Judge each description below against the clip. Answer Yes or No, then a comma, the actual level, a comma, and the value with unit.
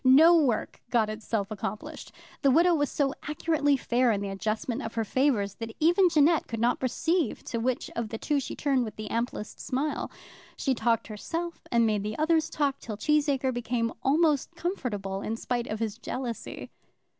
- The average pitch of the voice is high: Yes, very high, 250 Hz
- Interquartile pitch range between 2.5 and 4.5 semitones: No, average, 4.9 semitones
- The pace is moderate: Yes, average, 180 wpm